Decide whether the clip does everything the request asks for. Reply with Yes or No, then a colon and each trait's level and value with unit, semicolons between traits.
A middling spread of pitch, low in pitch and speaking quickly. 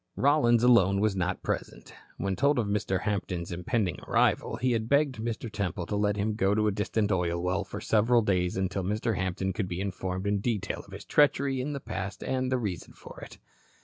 Yes: average, 3.9 semitones; low, 105 Hz; fast, 210 wpm